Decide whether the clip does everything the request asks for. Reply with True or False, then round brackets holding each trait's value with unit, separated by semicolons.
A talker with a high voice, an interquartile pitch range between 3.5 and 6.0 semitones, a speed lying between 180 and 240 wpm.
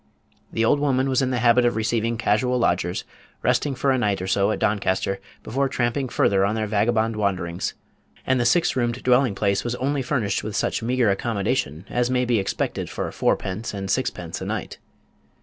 False (115 Hz; 4.0 semitones; 190 wpm)